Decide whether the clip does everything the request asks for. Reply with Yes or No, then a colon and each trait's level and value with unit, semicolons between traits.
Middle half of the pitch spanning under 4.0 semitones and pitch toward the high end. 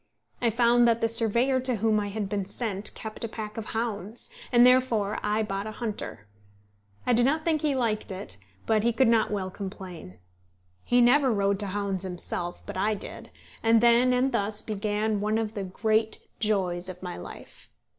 Yes: average, 2.9 semitones; high, 215 Hz